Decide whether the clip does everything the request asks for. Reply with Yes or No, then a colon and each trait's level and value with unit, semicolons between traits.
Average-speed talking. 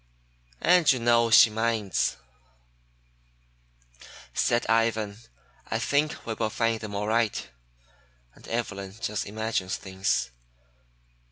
No: slow, 105 wpm